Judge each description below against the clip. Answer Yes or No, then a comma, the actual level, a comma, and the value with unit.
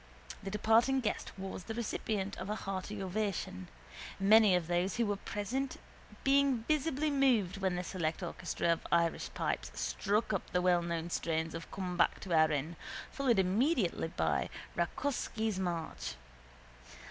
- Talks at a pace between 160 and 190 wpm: No, average, 145 wpm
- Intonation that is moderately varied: Yes, average, 4.5 semitones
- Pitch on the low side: No, high, 195 Hz